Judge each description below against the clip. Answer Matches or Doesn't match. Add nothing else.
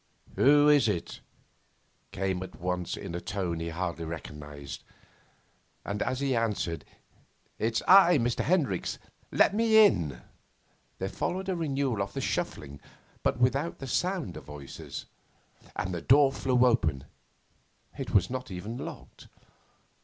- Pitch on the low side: Matches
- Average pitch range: Doesn't match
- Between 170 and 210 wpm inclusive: Doesn't match